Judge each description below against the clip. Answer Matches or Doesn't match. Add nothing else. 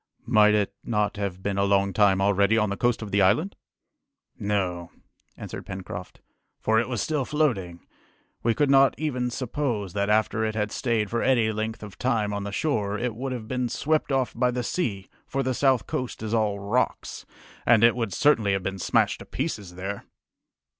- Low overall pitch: Matches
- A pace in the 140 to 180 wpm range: Doesn't match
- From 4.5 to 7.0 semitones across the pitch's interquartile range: Doesn't match